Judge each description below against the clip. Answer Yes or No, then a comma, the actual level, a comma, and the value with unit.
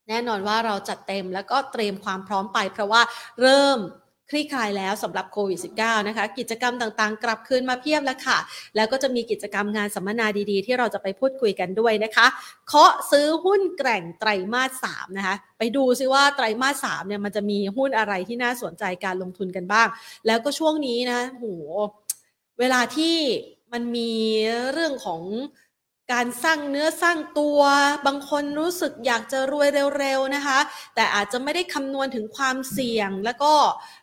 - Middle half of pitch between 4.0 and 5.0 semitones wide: Yes, average, 4.7 semitones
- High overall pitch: Yes, high, 240 Hz